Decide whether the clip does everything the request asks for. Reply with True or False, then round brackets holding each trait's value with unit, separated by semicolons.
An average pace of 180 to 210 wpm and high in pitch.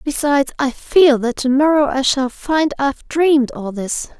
False (170 wpm; 275 Hz)